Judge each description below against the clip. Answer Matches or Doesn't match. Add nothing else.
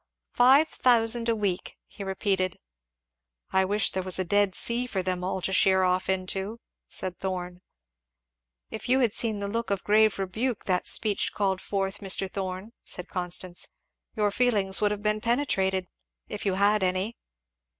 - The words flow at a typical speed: Matches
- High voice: Matches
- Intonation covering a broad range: Doesn't match